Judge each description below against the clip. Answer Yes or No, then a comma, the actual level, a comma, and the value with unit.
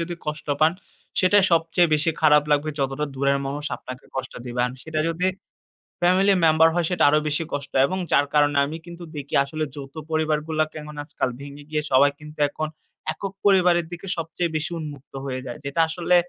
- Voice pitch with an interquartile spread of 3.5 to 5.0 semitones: No, average, 2.7 semitones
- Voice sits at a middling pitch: Yes, medium, 155 Hz